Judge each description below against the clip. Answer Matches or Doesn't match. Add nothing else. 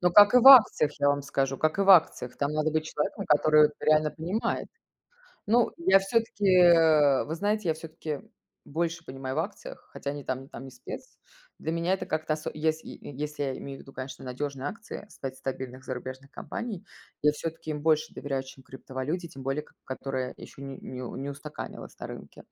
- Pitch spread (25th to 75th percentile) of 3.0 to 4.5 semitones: Matches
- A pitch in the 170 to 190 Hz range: Doesn't match